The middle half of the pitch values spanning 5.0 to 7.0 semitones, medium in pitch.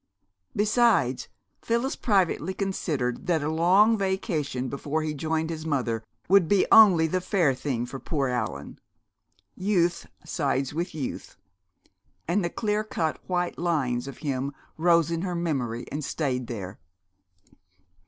Yes: average, 5.3 semitones; medium, 160 Hz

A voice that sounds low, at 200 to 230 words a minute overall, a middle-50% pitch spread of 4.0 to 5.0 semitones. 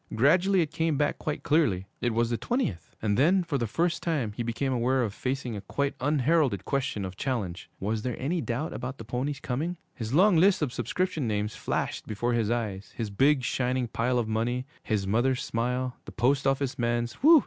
Yes: low, 125 Hz; fast, 205 wpm; average, 4.5 semitones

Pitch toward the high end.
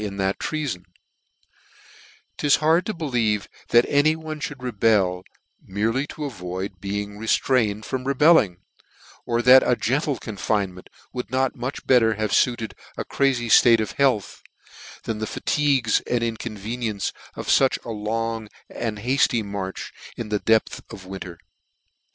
No: low, 115 Hz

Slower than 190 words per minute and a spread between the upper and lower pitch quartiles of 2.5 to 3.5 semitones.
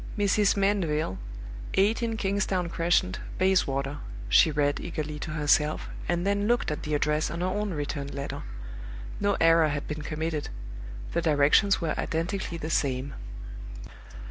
No: average, 140 wpm; average, 4.5 semitones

